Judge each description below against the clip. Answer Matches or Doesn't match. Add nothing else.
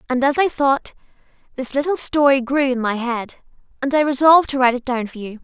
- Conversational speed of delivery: Doesn't match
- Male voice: Doesn't match